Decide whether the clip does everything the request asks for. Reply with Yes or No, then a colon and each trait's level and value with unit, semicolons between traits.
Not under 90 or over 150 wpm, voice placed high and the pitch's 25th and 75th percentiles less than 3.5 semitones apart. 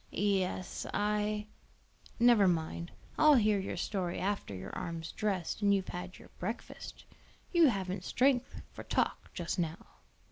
Yes: average, 145 wpm; high, 195 Hz; average, 3.1 semitones